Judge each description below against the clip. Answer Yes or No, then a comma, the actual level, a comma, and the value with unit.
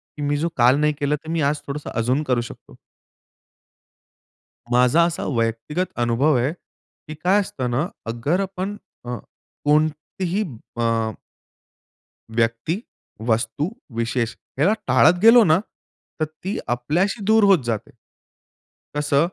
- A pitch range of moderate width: No, wide, 5.9 semitones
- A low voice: No, medium, 145 Hz